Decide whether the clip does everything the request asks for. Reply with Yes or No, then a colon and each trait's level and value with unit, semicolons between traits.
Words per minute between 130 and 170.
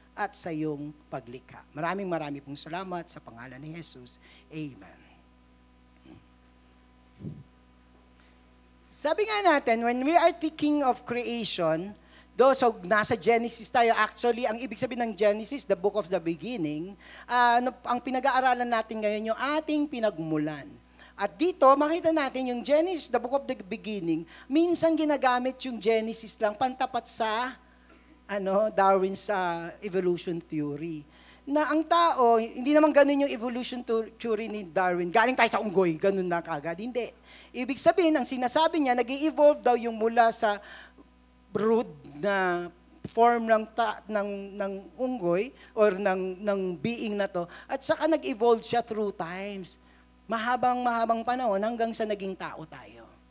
Yes: average, 145 wpm